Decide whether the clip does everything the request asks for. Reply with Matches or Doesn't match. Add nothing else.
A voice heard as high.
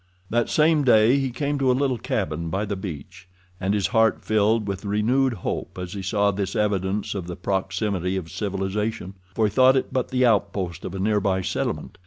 Doesn't match